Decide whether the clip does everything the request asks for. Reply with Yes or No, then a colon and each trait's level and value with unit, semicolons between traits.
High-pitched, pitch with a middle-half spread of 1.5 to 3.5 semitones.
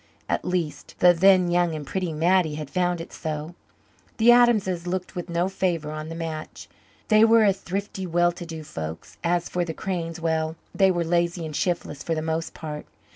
No: medium, 175 Hz; narrow, 2.4 semitones